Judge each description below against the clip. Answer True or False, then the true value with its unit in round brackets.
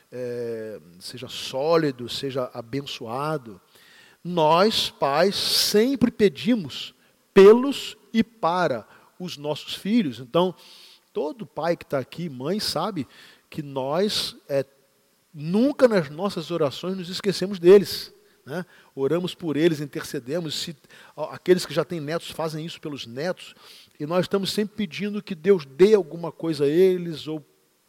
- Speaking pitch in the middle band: True (165 Hz)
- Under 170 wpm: True (130 wpm)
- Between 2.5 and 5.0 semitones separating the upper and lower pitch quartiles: False (5.6 semitones)